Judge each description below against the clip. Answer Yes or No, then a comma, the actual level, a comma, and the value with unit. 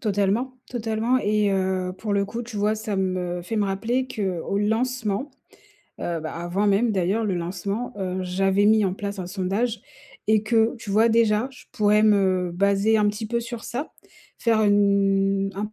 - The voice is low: No, high, 205 Hz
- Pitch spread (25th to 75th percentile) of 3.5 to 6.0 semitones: No, narrow, 2.5 semitones